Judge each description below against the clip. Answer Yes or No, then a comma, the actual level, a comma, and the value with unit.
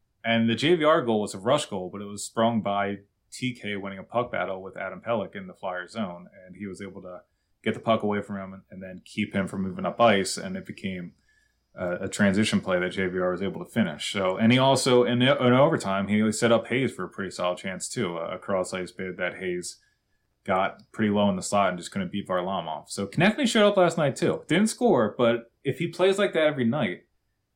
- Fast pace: Yes, fast, 235 wpm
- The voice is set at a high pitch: No, low, 105 Hz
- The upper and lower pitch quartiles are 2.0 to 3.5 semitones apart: No, average, 4.8 semitones